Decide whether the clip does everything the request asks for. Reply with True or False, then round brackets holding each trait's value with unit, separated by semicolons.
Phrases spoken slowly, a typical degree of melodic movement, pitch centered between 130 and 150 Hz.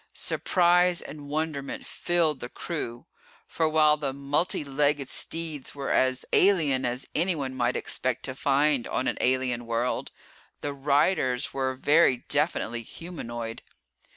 True (130 wpm; 3.4 semitones; 140 Hz)